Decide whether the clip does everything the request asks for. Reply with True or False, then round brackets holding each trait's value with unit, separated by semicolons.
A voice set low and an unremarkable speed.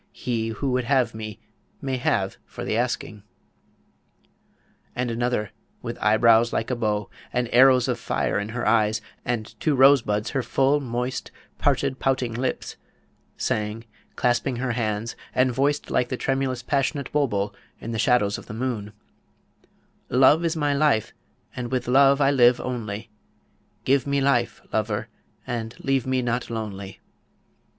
True (120 Hz; 150 wpm)